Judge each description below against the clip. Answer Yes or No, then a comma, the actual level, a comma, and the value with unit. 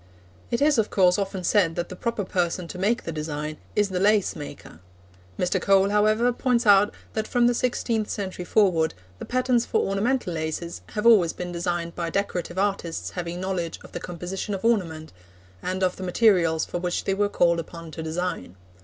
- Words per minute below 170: No, average, 190 wpm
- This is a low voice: No, medium, 185 Hz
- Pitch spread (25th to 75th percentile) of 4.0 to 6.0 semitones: No, average, 3.5 semitones